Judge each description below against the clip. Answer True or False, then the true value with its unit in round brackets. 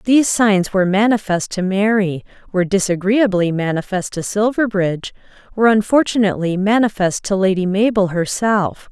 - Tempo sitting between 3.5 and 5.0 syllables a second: False (5.3 syllables/s)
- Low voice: False (200 Hz)